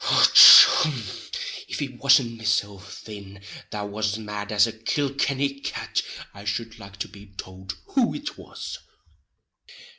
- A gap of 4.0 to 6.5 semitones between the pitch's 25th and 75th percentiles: Yes, average, 5.0 semitones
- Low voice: Yes, low, 110 Hz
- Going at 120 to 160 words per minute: Yes, average, 140 wpm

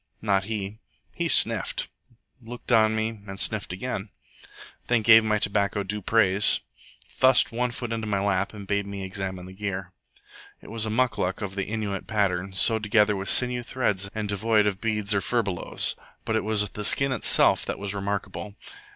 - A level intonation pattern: Yes, narrow, 2.2 semitones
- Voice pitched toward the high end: No, low, 105 Hz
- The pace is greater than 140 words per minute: Yes, average, 175 wpm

